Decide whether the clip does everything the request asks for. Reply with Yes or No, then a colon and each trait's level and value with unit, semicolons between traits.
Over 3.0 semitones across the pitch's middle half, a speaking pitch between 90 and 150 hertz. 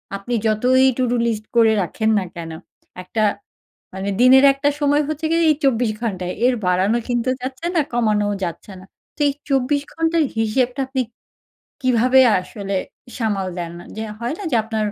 No: average, 4.0 semitones; high, 235 Hz